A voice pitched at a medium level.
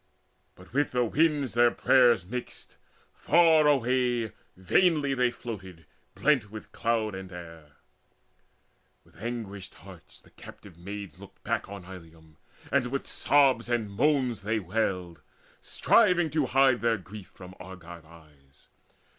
No: low, 110 Hz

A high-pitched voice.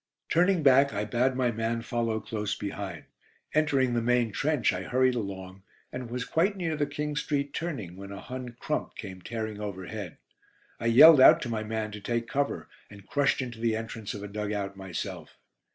No: low, 115 Hz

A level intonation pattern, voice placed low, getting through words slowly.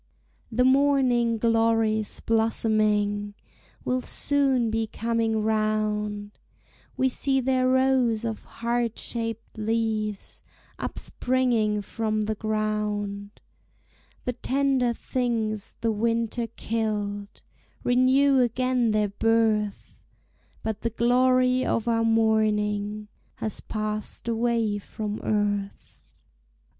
No: narrow, 2.3 semitones; high, 225 Hz; slow, 95 wpm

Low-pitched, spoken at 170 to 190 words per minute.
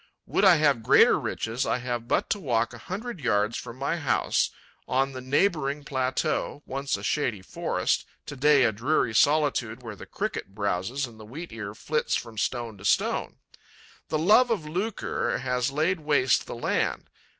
Yes: low, 130 Hz; average, 175 wpm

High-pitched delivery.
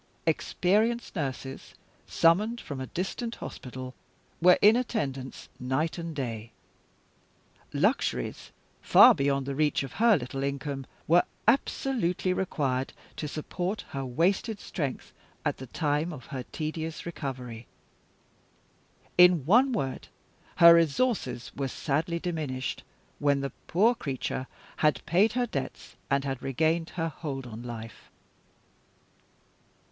No: medium, 150 Hz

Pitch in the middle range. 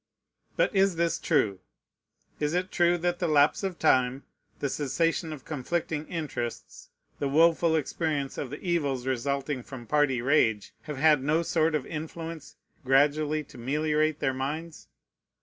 Yes: medium, 150 Hz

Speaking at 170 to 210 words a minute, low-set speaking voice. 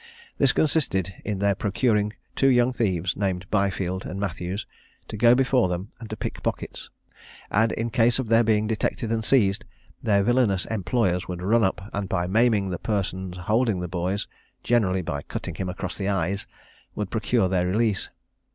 Yes: average, 175 wpm; low, 100 Hz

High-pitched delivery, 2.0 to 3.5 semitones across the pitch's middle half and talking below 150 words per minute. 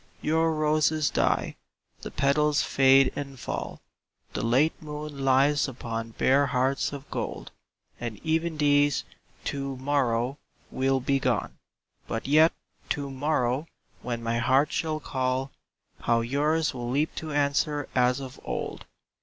No: medium, 140 Hz; average, 2.7 semitones; slow, 135 wpm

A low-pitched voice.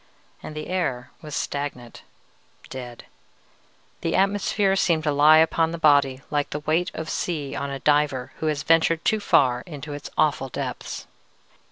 No: medium, 150 Hz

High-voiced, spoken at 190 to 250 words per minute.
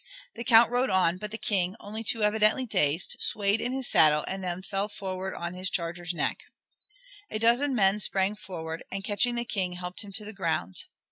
Yes: high, 195 Hz; average, 200 wpm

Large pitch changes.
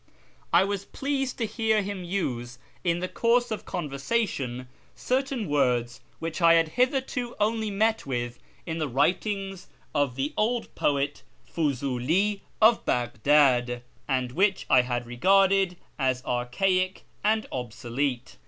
Yes: wide, 8.5 semitones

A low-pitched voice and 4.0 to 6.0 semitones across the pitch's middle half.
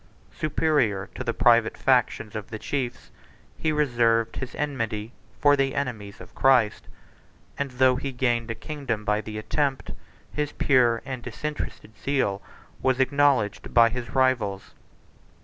No: low, 125 Hz; average, 3.5 semitones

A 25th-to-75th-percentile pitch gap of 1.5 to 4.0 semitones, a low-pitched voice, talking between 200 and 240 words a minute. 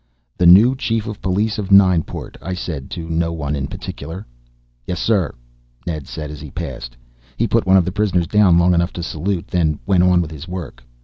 Yes: average, 3.5 semitones; very low, 90 Hz; fast, 205 wpm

